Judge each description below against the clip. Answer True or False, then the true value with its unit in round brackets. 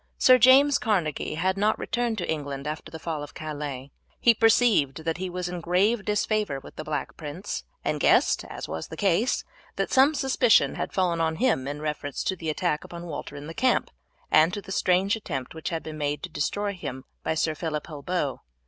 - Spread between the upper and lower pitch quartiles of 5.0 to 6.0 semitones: True (5.4 semitones)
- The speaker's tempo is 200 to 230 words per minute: True (205 wpm)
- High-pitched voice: False (170 Hz)